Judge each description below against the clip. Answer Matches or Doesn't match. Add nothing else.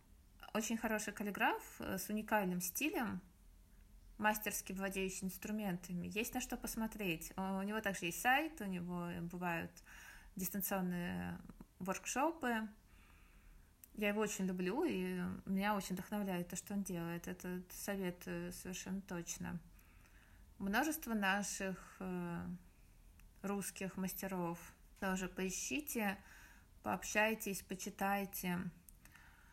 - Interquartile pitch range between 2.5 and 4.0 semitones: Matches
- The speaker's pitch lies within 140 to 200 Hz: Matches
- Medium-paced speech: Doesn't match